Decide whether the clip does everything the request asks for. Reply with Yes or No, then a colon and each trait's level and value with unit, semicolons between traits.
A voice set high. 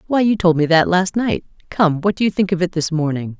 No: medium, 175 Hz